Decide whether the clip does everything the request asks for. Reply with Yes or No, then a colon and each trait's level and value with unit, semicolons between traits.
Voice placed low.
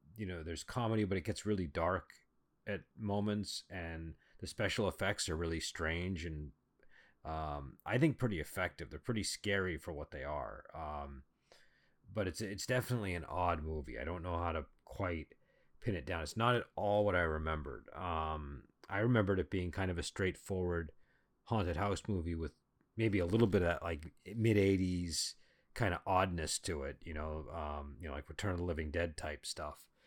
Yes: very low, 85 Hz